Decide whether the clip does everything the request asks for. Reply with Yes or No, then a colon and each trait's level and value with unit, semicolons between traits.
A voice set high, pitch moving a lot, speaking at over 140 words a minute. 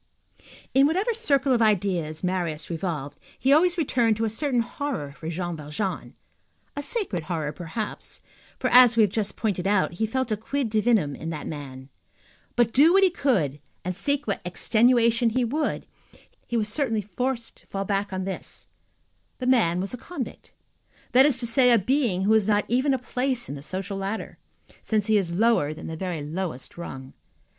Yes: high, 215 Hz; wide, 6.1 semitones; average, 185 wpm